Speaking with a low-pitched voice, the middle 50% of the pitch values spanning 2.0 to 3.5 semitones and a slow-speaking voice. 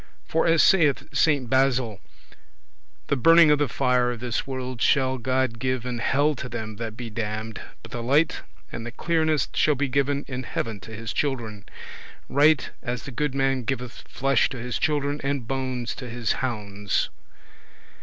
No: low, 130 Hz; average, 3.2 semitones; average, 175 wpm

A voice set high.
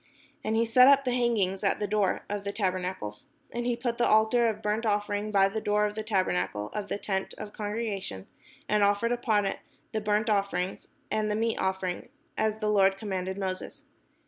Yes: high, 210 Hz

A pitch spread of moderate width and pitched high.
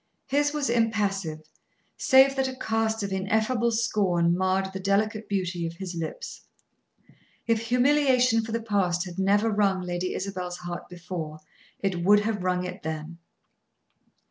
Yes: average, 4.0 semitones; high, 200 Hz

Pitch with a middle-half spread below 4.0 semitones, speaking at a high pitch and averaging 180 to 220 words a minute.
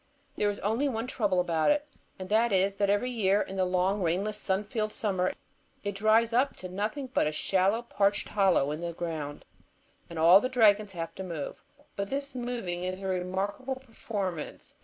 Yes: average, 3.5 semitones; high, 200 Hz; average, 190 wpm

